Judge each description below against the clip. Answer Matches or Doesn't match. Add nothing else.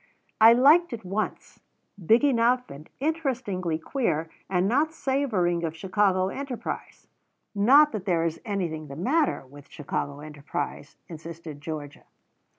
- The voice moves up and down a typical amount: Doesn't match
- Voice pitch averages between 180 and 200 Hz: Matches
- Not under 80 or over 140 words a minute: Matches